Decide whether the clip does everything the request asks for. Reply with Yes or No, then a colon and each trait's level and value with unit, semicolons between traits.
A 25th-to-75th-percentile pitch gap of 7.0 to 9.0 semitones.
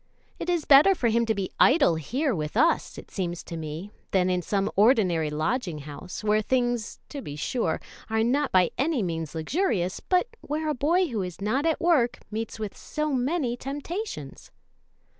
Yes: wide, 8.1 semitones